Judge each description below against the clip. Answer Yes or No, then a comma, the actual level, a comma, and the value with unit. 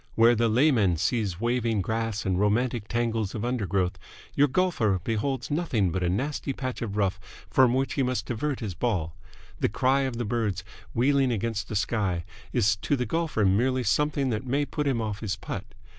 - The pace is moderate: Yes, average, 190 wpm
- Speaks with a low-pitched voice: Yes, low, 115 Hz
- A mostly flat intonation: No, average, 4.1 semitones